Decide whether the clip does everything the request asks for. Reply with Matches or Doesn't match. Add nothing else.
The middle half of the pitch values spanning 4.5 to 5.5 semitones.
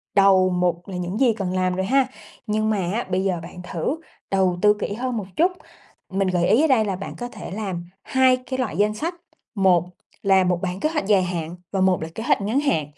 Doesn't match